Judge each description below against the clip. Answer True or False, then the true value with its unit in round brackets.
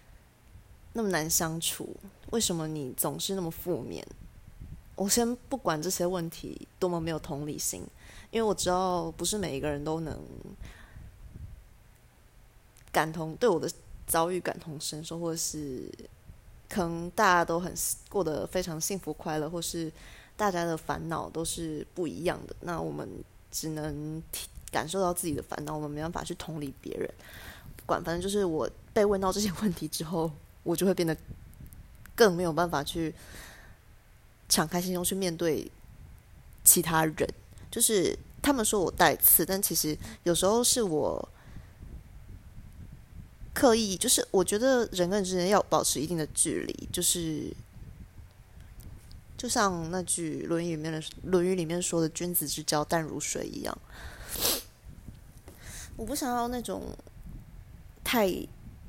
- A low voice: False (170 Hz)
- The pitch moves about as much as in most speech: True (3.2 semitones)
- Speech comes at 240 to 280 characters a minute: False (215 characters per minute)